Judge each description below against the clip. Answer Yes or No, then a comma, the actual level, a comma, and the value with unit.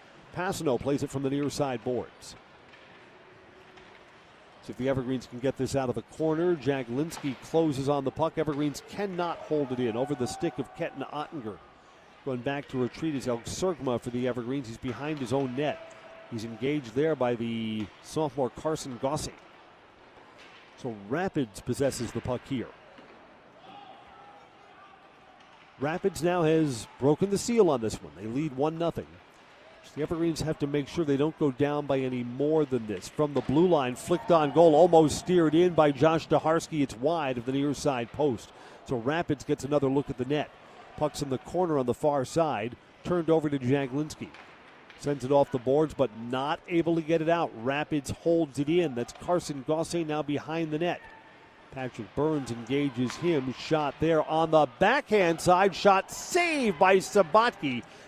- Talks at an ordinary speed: Yes, average, 175 wpm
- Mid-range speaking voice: Yes, medium, 145 Hz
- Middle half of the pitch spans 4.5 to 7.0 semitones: No, average, 4.0 semitones